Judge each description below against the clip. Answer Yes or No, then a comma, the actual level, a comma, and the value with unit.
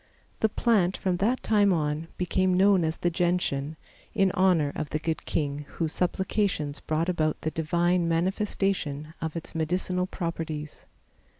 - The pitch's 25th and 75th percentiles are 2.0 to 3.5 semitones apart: Yes, average, 3.1 semitones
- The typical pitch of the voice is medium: Yes, medium, 170 Hz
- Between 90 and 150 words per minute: Yes, average, 145 wpm